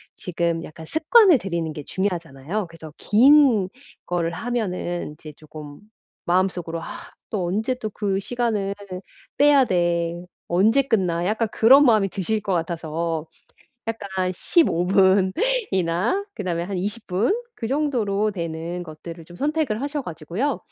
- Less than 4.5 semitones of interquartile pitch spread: No, average, 5.1 semitones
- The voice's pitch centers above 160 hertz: Yes, high, 190 Hz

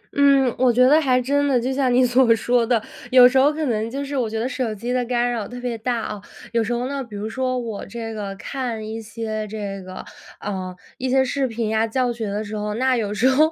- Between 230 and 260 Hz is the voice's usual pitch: Yes, high, 240 Hz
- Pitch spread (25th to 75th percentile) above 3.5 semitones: No, average, 2.9 semitones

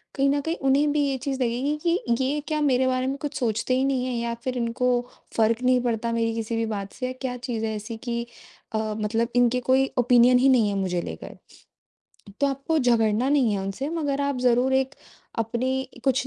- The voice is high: Yes, very high, 250 Hz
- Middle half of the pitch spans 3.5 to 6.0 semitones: No, average, 2.8 semitones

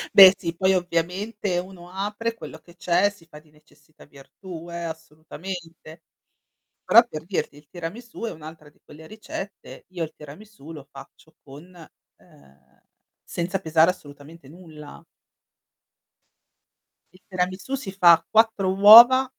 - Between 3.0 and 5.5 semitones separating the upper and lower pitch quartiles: Yes, average, 3.6 semitones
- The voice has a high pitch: No, medium, 175 Hz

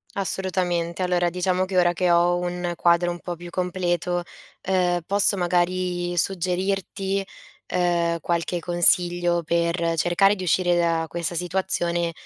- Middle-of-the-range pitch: Yes, medium, 175 Hz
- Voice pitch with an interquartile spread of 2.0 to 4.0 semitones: No, narrow, 1.0 semitones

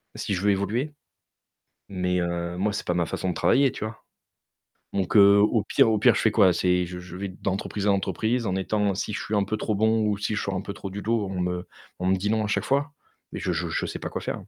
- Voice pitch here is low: Yes, low, 100 Hz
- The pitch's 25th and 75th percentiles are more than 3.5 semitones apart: No, average, 2.8 semitones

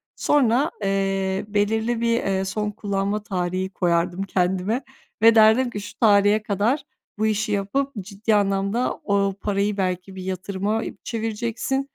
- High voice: Yes, high, 205 Hz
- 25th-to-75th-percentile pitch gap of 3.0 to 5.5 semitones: No, narrow, 2.4 semitones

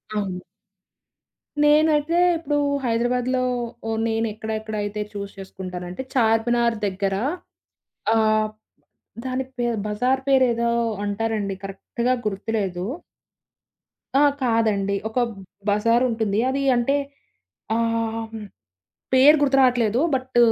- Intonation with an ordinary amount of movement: Yes, average, 3.3 semitones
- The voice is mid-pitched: No, high, 225 Hz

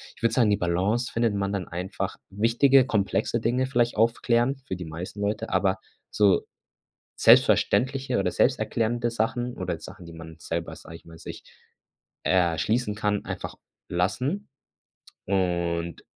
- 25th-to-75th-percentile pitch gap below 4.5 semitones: No, average, 4.9 semitones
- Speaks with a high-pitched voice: No, low, 105 Hz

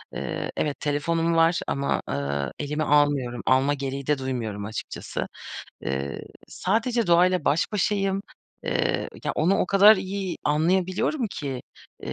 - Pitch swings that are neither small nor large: No, wide, 5.8 semitones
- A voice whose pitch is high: No, medium, 155 Hz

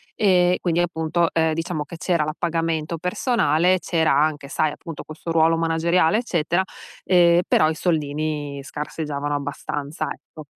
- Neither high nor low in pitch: Yes, medium, 160 Hz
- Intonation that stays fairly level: Yes, narrow, 2.3 semitones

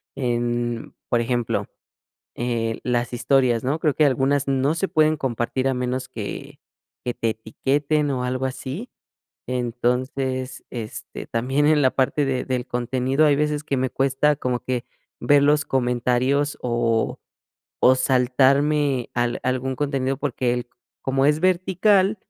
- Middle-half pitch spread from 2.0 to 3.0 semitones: Yes, average, 2.7 semitones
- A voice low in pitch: Yes, low, 130 Hz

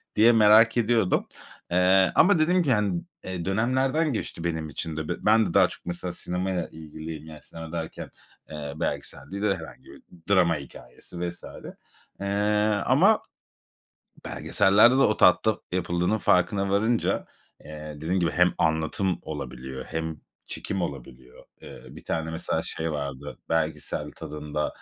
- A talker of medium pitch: No, very low, 90 Hz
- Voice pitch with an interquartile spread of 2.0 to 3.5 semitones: No, average, 5.0 semitones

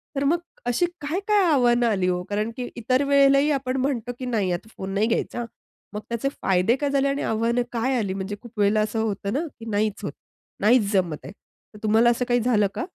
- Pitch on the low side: No, high, 235 Hz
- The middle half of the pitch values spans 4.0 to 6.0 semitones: Yes, average, 4.3 semitones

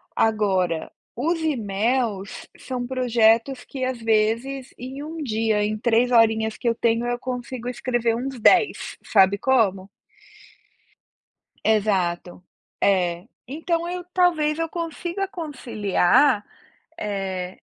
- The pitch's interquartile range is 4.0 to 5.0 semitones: Yes, average, 4.3 semitones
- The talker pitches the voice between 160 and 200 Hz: No, high, 235 Hz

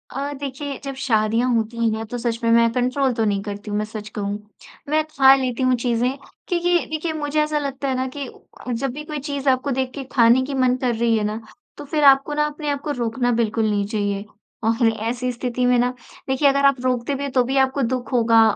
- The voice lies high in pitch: Yes, very high, 255 Hz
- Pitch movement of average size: Yes, average, 3.4 semitones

